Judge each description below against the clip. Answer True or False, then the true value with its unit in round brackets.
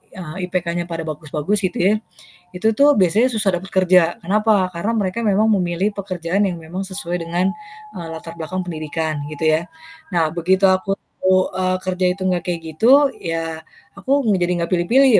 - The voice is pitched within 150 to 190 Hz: True (185 Hz)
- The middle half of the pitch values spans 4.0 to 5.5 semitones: False (2.8 semitones)